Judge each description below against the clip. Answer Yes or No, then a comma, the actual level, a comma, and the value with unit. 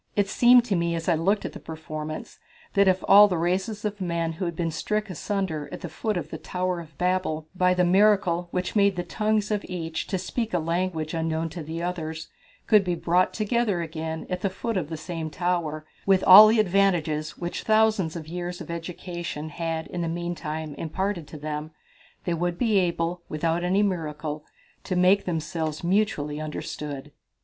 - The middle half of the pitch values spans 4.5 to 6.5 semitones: No, average, 3.1 semitones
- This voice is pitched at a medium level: Yes, medium, 175 Hz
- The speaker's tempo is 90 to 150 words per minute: No, average, 190 wpm